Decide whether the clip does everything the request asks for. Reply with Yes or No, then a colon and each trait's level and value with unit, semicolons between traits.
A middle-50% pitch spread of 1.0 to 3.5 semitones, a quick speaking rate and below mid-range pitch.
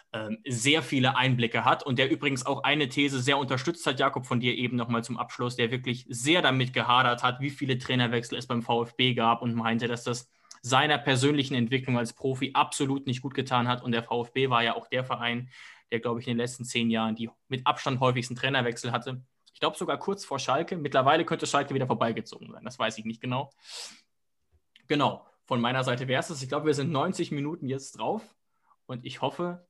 Yes: average, 2.7 semitones; fast, 210 wpm; low, 130 Hz